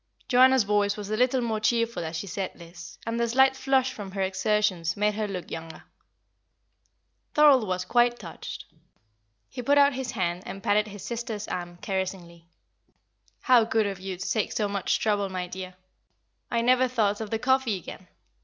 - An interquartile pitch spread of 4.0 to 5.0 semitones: Yes, average, 4.3 semitones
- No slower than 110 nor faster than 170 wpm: No, average, 180 wpm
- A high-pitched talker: Yes, high, 210 Hz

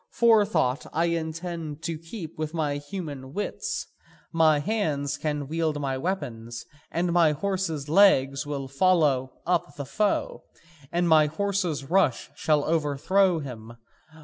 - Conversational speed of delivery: No, slow, 125 wpm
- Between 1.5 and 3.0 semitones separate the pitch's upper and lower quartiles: No, average, 3.6 semitones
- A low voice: No, medium, 155 Hz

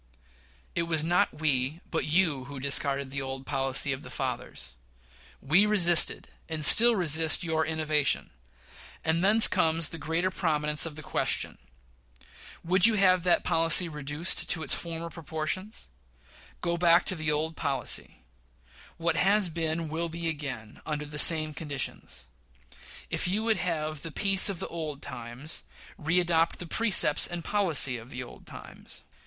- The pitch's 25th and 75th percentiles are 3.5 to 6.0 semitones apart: No, average, 2.8 semitones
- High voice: No, medium, 160 Hz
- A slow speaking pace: No, average, 155 wpm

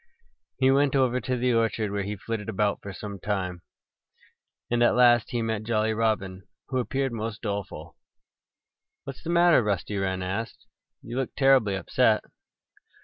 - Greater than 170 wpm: No, average, 155 wpm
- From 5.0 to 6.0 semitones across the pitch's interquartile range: No, average, 3.7 semitones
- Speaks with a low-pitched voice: Yes, low, 110 Hz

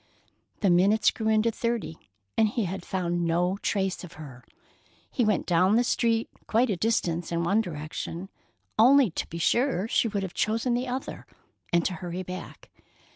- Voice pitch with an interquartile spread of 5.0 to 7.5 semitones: No, average, 4.6 semitones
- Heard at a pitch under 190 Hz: No, high, 195 Hz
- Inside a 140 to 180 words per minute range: Yes, average, 175 wpm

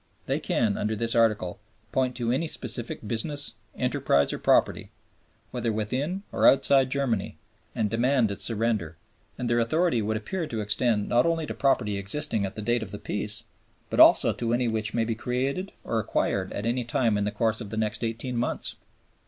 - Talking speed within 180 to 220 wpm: Yes, average, 190 wpm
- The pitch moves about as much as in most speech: Yes, average, 3.2 semitones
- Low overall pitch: Yes, low, 115 Hz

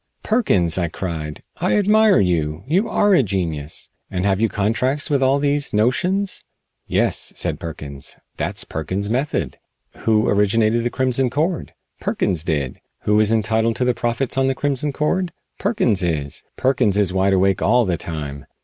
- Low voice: Yes, low, 110 Hz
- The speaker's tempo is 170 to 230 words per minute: No, average, 160 wpm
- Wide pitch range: Yes, wide, 7.0 semitones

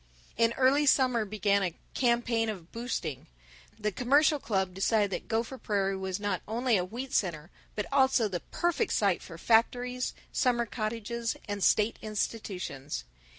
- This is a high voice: Yes, high, 220 Hz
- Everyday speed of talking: Yes, average, 150 wpm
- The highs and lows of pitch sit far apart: No, average, 3.9 semitones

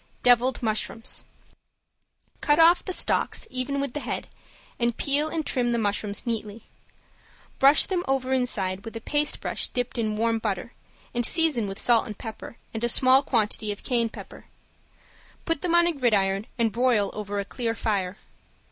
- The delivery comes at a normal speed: Yes, average, 170 wpm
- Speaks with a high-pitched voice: Yes, high, 235 Hz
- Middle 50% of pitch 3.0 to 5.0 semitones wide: Yes, average, 3.9 semitones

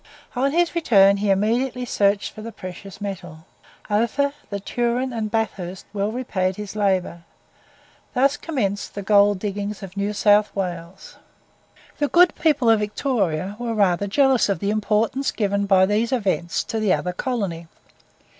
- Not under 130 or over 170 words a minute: Yes, average, 155 wpm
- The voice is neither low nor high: No, high, 205 Hz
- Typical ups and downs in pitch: Yes, average, 3.4 semitones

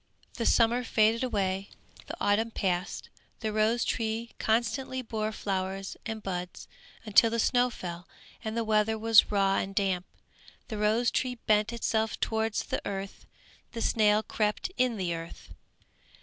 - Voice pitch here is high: Yes, high, 215 Hz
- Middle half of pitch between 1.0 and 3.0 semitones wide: Yes, average, 2.7 semitones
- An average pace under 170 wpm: Yes, average, 150 wpm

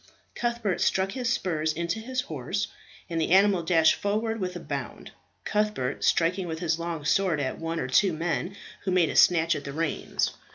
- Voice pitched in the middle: Yes, medium, 175 Hz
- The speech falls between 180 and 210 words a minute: Yes, average, 190 wpm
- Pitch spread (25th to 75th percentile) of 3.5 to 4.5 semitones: Yes, average, 3.8 semitones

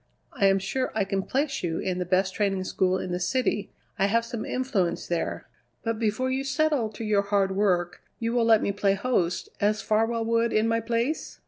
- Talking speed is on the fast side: Yes, fast, 210 wpm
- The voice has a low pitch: No, high, 215 Hz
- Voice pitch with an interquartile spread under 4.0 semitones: Yes, average, 3.2 semitones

